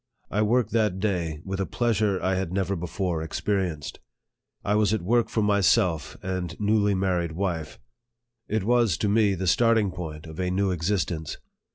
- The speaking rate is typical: Yes, average, 170 wpm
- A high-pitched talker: No, very low, 95 Hz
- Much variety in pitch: No, average, 3.2 semitones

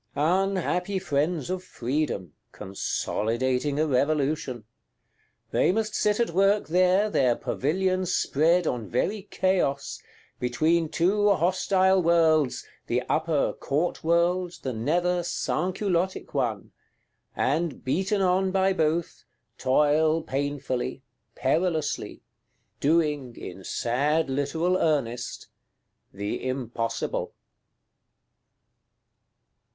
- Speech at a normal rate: No, slow, 90 wpm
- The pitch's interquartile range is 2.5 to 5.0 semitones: No, wide, 5.5 semitones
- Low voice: No, medium, 160 Hz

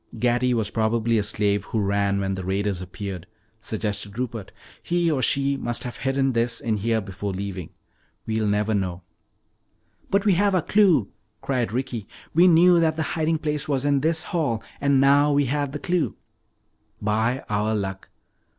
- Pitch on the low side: Yes, low, 115 Hz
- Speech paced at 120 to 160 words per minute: No, average, 170 wpm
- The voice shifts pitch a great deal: Yes, wide, 5.9 semitones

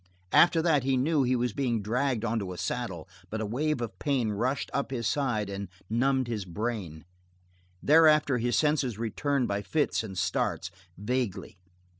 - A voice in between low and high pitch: No, low, 120 Hz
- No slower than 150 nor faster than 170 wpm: Yes, average, 165 wpm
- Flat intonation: No, average, 4.7 semitones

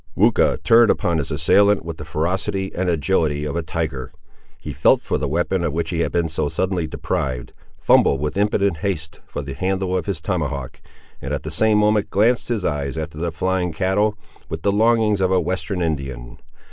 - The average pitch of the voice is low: Yes, very low, 85 Hz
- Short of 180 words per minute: No, average, 195 wpm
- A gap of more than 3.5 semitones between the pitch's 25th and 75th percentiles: Yes, average, 4.3 semitones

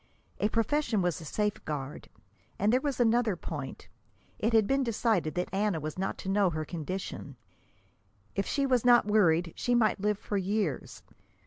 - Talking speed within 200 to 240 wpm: No, average, 170 wpm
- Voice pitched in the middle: No, high, 205 Hz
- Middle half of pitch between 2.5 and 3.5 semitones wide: No, average, 4.6 semitones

